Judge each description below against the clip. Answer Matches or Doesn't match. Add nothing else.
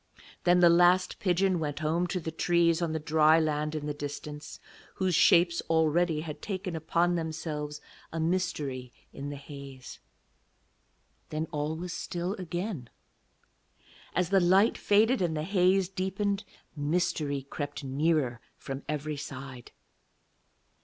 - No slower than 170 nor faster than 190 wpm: Doesn't match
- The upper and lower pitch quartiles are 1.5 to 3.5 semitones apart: Matches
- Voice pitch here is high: Doesn't match